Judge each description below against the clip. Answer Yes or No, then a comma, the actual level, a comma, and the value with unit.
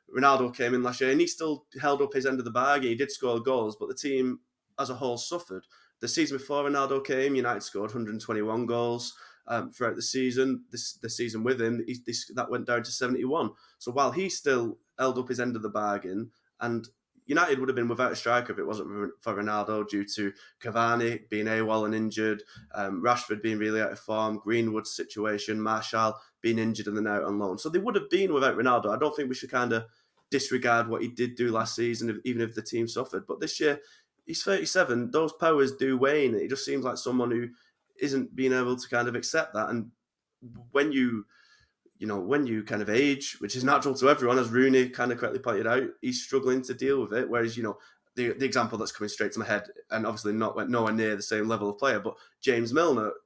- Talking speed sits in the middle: No, fast, 225 wpm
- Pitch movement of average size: Yes, average, 3.1 semitones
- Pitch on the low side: Yes, low, 120 Hz